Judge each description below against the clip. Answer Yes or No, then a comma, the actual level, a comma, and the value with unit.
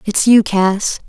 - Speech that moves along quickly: No, average, 165 wpm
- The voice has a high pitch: Yes, high, 205 Hz